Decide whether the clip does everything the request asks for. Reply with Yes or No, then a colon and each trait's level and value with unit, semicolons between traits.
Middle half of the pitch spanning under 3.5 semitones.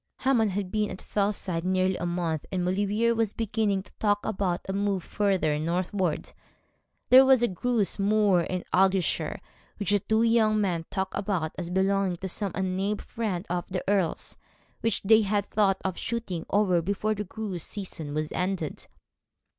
Yes: average, 2.7 semitones